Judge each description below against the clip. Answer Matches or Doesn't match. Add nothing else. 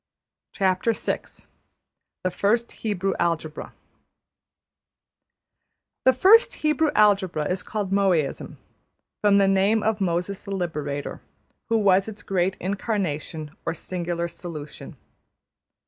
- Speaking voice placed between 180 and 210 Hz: Matches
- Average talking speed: Doesn't match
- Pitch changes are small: Doesn't match